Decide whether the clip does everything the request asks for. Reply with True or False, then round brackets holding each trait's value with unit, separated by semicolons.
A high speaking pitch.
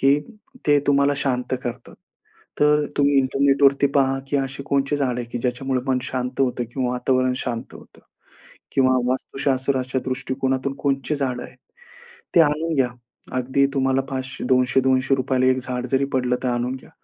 False (130 Hz)